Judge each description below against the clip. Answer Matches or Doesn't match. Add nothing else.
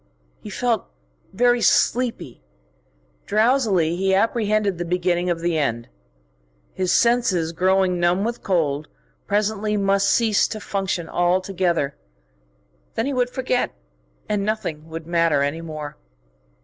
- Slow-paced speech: Matches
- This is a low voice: Doesn't match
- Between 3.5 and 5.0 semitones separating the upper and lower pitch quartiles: Matches